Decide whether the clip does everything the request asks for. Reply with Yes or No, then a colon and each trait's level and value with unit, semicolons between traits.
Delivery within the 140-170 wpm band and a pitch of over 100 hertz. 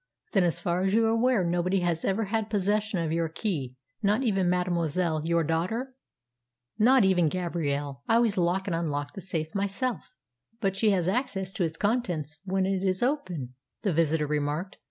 No: average, 180 wpm; medium, 185 Hz